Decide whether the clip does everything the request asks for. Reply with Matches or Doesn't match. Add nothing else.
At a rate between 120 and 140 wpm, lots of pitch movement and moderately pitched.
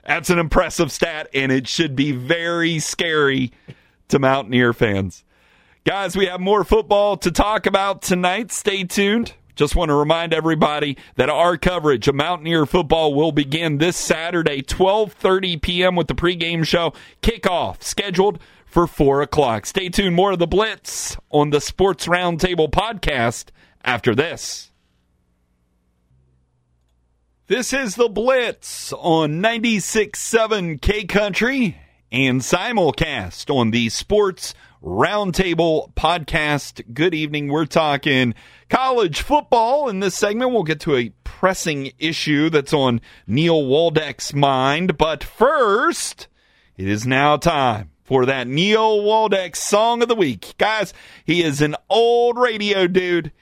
Matches